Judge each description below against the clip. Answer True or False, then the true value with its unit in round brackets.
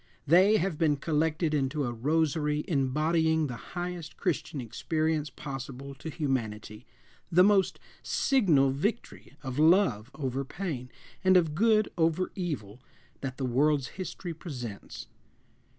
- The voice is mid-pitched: True (150 Hz)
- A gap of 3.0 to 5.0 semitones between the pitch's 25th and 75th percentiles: True (4.3 semitones)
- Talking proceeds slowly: True (125 wpm)